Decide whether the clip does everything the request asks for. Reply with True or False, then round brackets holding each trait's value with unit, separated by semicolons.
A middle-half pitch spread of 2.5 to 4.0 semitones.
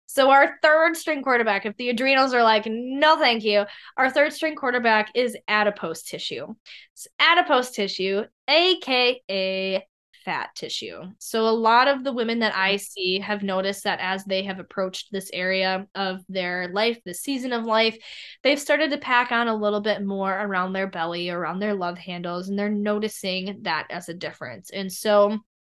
False (4.8 semitones)